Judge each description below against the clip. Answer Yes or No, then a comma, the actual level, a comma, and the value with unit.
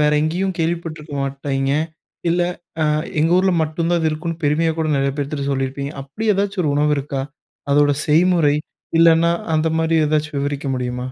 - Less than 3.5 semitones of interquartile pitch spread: Yes, average, 2.9 semitones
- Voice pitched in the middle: Yes, medium, 155 Hz